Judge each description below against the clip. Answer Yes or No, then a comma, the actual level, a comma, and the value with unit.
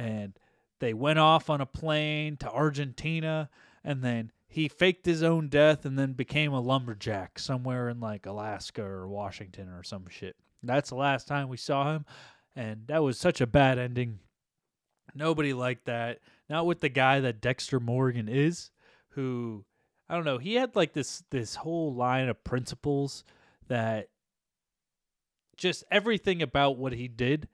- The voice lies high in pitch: No, low, 135 Hz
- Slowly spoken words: No, average, 165 wpm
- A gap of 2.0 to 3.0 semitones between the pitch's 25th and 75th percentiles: No, average, 4.4 semitones